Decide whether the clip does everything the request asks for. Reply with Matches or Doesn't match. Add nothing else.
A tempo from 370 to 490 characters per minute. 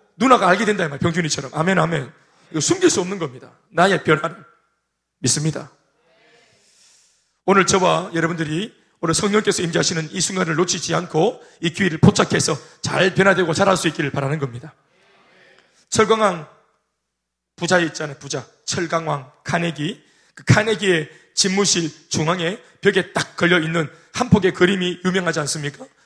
Doesn't match